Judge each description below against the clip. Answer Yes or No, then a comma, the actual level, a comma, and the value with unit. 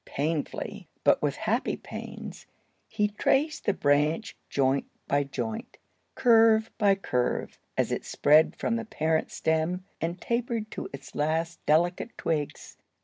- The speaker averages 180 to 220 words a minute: No, slow, 135 wpm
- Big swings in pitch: Yes, wide, 6.6 semitones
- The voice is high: No, medium, 170 Hz